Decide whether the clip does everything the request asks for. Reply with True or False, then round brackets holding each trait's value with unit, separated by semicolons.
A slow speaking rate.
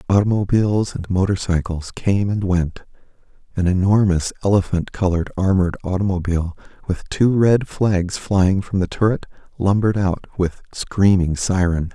True (125 wpm)